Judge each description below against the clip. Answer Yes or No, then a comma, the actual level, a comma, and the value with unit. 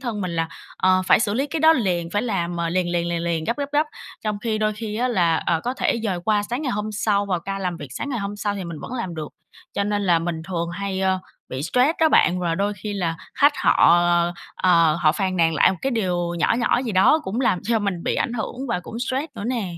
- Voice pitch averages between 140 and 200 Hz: Yes, high, 195 Hz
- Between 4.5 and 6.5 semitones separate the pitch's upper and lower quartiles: Yes, average, 4.8 semitones